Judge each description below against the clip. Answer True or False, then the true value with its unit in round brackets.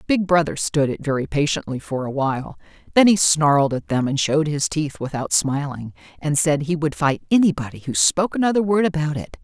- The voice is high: False (150 Hz)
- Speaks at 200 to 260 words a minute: True (205 wpm)